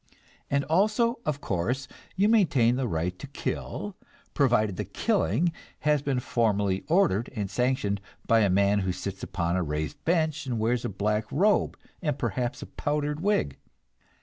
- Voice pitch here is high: No, low, 125 Hz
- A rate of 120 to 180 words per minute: Yes, average, 160 wpm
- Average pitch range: No, wide, 7.1 semitones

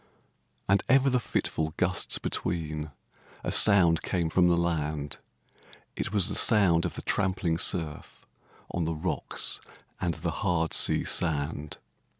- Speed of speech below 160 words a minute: Yes, average, 140 wpm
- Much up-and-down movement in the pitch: No, average, 3.0 semitones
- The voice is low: Yes, very low, 85 Hz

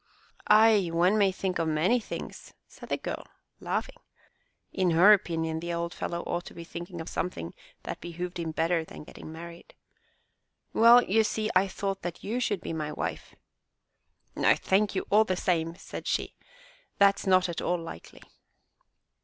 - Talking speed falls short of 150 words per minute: No, average, 170 wpm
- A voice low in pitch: No, medium, 175 Hz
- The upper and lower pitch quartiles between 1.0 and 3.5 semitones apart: Yes, average, 3.1 semitones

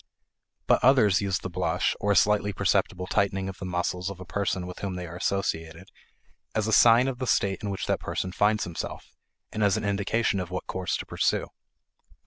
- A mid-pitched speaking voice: No, very low, 95 Hz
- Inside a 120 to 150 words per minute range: No, fast, 205 wpm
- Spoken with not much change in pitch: Yes, narrow, 2.1 semitones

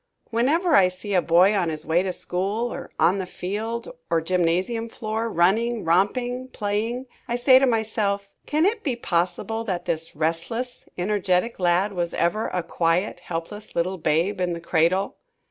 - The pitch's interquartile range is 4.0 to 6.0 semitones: Yes, average, 4.7 semitones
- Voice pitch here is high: Yes, high, 195 Hz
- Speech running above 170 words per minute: No, average, 165 wpm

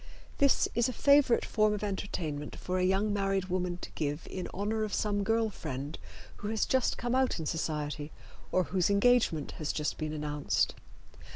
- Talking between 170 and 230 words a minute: Yes, average, 180 wpm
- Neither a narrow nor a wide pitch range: No, wide, 5.7 semitones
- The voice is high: Yes, high, 195 Hz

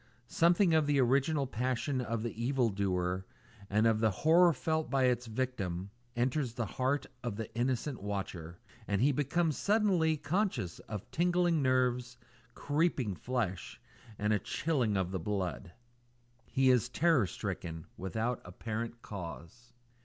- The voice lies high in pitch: No, low, 125 Hz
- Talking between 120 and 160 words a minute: Yes, average, 140 wpm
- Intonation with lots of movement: Yes, wide, 5.8 semitones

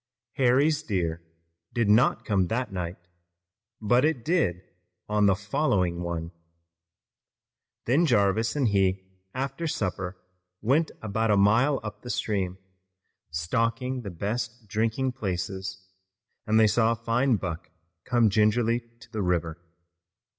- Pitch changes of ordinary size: Yes, average, 4.5 semitones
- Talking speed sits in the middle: No, slow, 125 wpm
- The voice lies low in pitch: Yes, low, 110 Hz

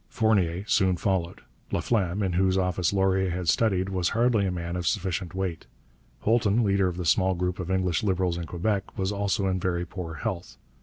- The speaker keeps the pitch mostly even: Yes, narrow, 2.0 semitones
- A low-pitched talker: Yes, very low, 95 Hz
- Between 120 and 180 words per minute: No, average, 190 wpm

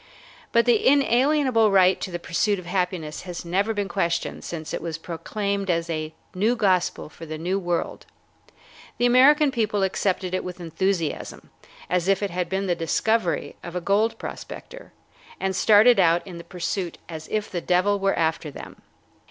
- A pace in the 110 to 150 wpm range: No, average, 175 wpm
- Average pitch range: Yes, average, 3.5 semitones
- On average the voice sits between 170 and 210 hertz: Yes, medium, 185 Hz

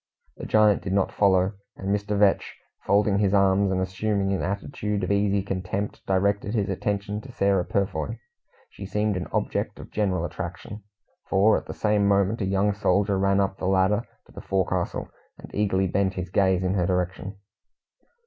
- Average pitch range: No, narrow, 1.4 semitones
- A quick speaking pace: No, average, 175 wpm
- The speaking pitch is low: Yes, low, 100 Hz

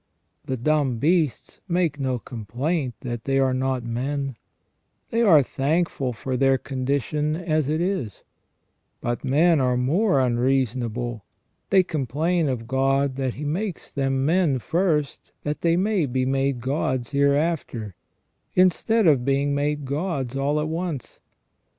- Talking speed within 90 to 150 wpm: Yes, average, 140 wpm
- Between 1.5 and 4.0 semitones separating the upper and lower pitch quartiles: Yes, average, 3.6 semitones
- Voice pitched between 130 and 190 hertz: Yes, medium, 140 Hz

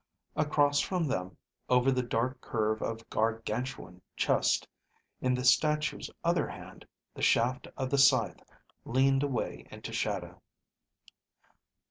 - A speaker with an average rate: No, slow, 120 wpm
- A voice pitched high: No, low, 130 Hz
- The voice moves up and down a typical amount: Yes, average, 3.2 semitones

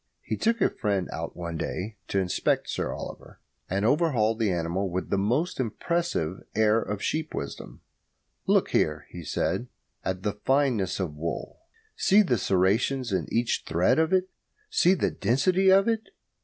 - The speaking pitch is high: No, low, 110 Hz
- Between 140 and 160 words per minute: No, average, 170 wpm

